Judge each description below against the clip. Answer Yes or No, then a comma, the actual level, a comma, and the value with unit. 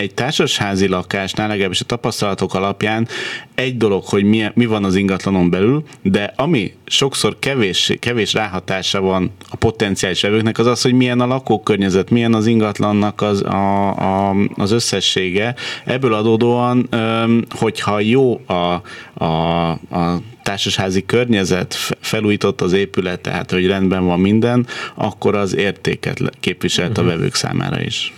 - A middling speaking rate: Yes, average, 135 wpm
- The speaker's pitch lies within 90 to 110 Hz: Yes, low, 105 Hz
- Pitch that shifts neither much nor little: Yes, average, 3.3 semitones